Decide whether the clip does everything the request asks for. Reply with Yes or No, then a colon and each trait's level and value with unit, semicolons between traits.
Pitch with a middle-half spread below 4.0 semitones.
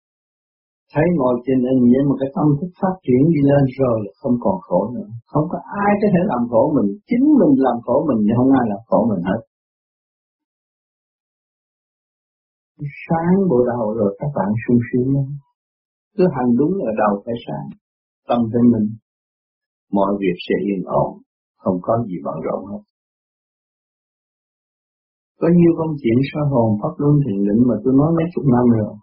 No: wide, 5.5 semitones